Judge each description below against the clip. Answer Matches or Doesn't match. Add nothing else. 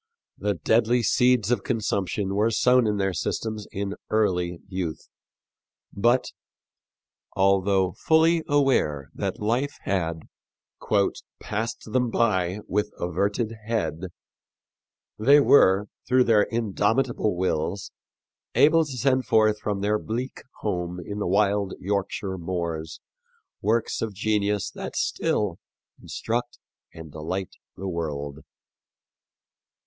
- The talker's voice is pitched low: Matches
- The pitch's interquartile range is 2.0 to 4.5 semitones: Matches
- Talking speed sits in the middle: Doesn't match